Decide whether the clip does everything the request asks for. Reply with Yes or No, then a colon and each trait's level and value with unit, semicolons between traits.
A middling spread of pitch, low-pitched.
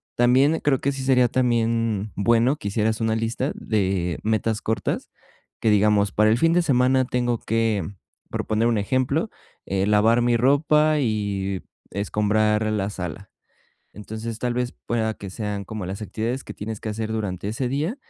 Yes: average, 3.0 semitones; low, 110 Hz